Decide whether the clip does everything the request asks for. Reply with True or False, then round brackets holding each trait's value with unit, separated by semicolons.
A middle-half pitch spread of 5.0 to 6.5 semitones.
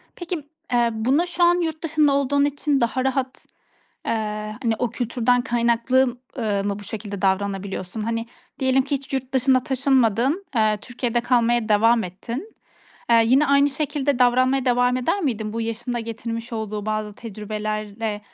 False (3.5 semitones)